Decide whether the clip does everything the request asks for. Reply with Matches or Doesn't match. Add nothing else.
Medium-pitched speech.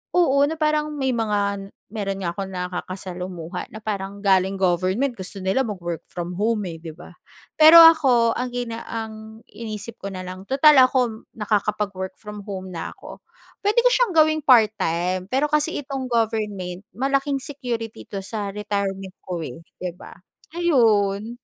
Doesn't match